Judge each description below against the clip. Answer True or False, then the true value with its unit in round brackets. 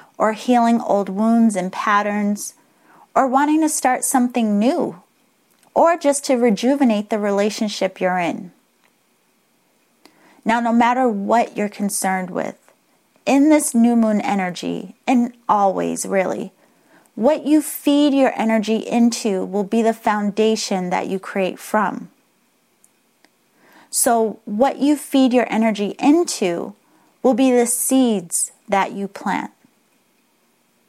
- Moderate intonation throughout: True (4.3 semitones)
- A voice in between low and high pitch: False (225 Hz)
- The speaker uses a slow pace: True (120 wpm)